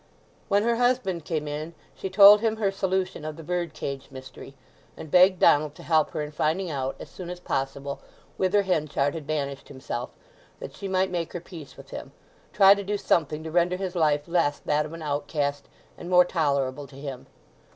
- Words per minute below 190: No, average, 200 wpm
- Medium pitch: Yes, medium, 160 Hz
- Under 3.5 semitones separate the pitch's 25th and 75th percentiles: No, average, 4.2 semitones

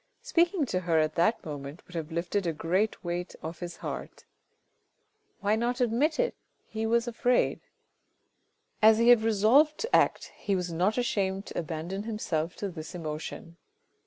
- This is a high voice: Yes, high, 195 Hz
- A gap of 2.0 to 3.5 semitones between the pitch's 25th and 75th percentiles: No, wide, 5.6 semitones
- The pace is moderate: Yes, average, 160 wpm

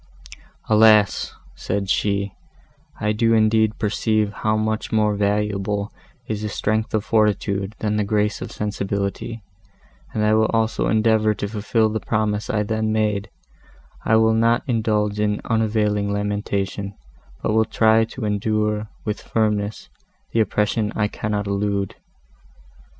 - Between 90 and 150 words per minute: Yes, slow, 135 wpm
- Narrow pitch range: Yes, narrow, 1.2 semitones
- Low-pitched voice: Yes, low, 105 Hz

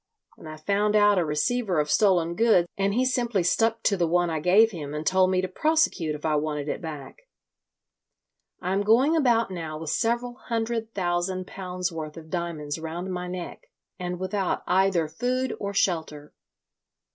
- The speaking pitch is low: No, medium, 185 Hz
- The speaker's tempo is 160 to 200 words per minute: Yes, average, 180 wpm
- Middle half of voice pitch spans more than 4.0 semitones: Yes, average, 5.1 semitones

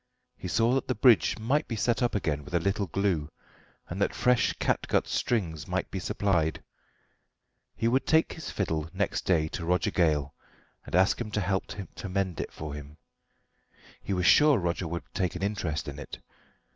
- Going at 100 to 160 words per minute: No, average, 185 wpm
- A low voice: Yes, very low, 95 Hz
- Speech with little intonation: No, wide, 5.5 semitones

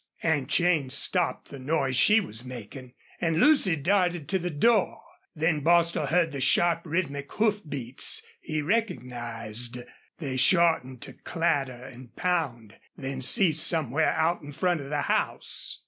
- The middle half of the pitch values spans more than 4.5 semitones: Yes, average, 4.9 semitones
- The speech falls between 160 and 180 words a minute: No, average, 145 wpm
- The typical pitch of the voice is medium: Yes, medium, 155 Hz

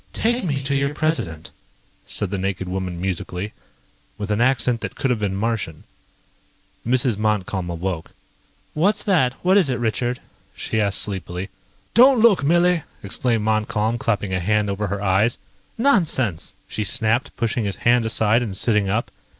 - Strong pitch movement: No, average, 5.0 semitones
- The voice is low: Yes, low, 110 Hz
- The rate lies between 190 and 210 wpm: No, average, 160 wpm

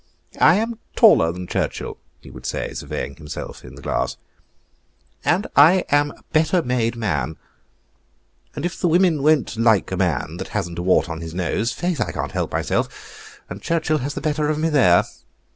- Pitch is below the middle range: Yes, low, 125 Hz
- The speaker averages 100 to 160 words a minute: No, average, 185 wpm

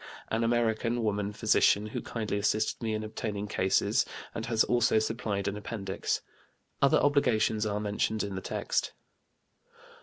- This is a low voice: Yes, low, 110 Hz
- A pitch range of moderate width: No, narrow, 1.8 semitones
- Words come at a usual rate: Yes, average, 145 wpm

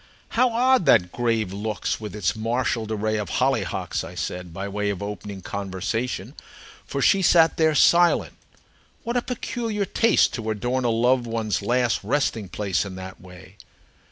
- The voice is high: No, low, 110 Hz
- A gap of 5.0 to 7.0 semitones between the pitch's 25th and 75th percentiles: Yes, wide, 5.5 semitones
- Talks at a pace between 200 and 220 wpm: No, average, 160 wpm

